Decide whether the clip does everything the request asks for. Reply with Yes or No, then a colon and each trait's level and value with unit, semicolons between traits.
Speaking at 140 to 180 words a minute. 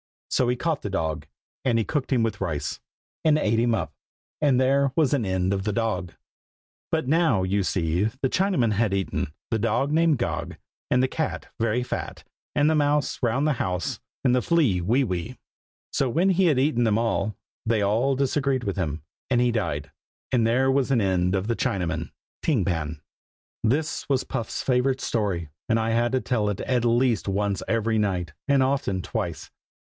No: average, 190 wpm